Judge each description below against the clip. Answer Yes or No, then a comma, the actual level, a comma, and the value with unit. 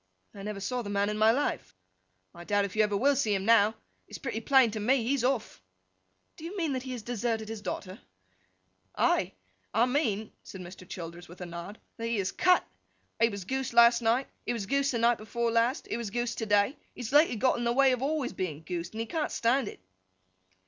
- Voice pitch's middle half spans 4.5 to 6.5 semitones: No, average, 3.9 semitones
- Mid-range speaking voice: No, high, 230 Hz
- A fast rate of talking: Yes, fast, 230 wpm